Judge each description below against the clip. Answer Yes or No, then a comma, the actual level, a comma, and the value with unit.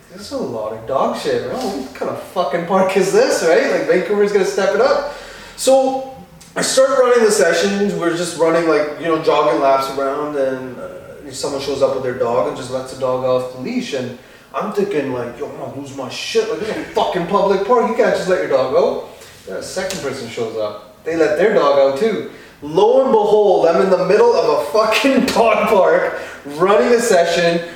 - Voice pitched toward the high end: Yes, high, 195 Hz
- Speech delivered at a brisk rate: Yes, fast, 225 wpm